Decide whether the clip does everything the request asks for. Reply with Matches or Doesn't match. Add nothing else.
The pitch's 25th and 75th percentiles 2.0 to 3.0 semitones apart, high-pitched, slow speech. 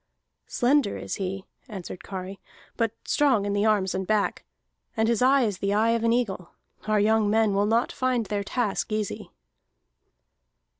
Doesn't match